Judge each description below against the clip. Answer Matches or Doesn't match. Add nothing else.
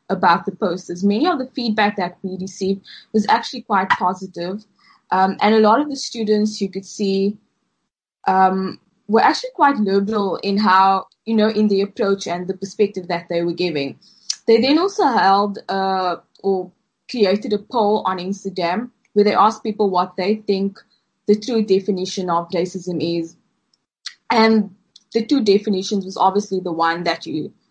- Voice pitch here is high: Matches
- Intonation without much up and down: Matches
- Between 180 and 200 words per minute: Doesn't match